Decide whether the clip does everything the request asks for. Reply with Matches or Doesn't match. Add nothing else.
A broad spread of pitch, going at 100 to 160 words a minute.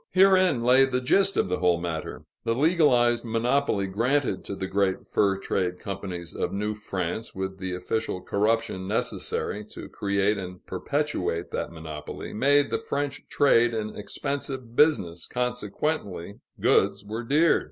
Matches